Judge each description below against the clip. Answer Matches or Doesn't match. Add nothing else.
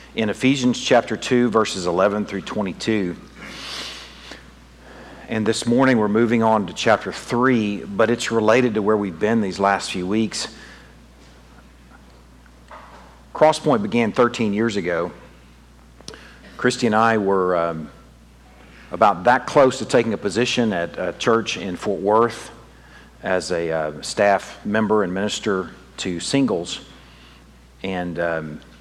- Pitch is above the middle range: Doesn't match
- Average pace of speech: Doesn't match